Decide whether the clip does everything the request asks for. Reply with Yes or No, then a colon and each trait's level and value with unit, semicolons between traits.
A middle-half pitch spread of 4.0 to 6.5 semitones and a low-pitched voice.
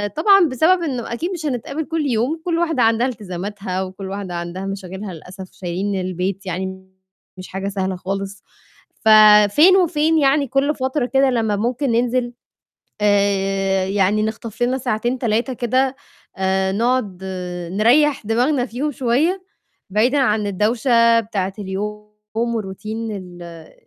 No: average, 5.1 semitones; high, 220 Hz